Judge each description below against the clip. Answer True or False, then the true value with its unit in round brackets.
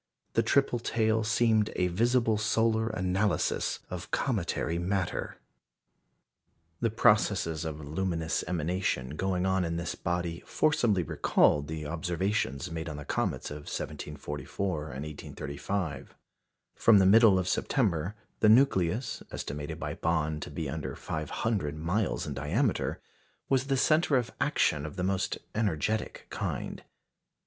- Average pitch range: False (5.9 semitones)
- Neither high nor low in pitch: False (90 Hz)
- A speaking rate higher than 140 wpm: False (135 wpm)